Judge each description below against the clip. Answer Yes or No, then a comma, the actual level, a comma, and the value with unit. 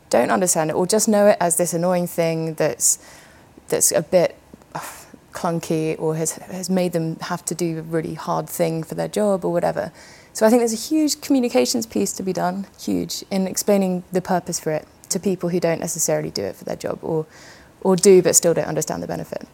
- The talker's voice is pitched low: No, medium, 180 Hz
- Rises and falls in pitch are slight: No, average, 3.0 semitones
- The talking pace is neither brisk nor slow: No, fast, 220 wpm